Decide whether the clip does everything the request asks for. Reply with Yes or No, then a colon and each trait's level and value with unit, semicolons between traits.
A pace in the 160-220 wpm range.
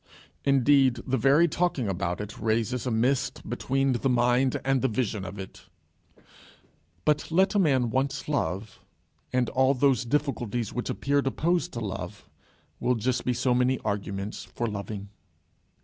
No: average, 150 wpm